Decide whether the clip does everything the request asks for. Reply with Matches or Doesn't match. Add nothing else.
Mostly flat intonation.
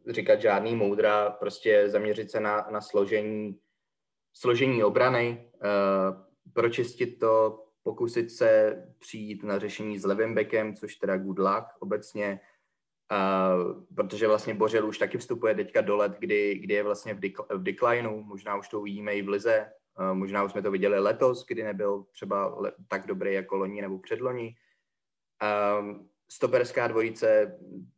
Matches